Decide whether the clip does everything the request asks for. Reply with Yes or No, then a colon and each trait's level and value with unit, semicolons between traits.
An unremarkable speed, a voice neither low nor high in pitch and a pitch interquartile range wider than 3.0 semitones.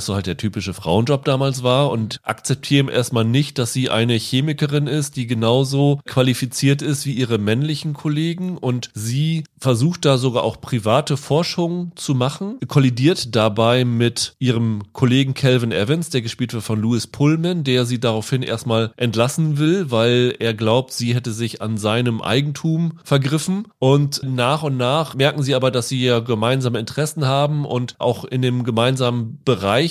No: average, 165 wpm; low, 130 Hz; average, 3.5 semitones